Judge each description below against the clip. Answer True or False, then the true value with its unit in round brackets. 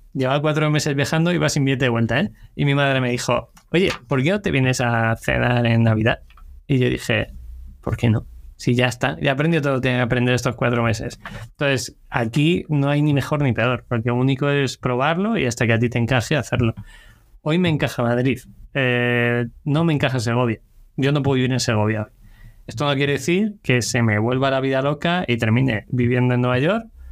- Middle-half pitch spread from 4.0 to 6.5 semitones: False (3.4 semitones)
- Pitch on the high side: False (125 Hz)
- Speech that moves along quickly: True (215 wpm)